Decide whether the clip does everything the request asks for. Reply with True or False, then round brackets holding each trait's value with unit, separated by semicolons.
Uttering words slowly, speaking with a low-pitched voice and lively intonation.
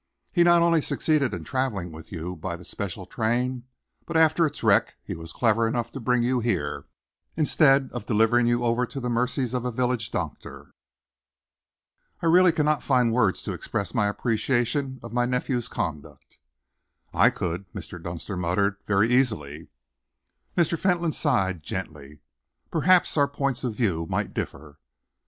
False (160 wpm; 120 Hz; 6.2 semitones)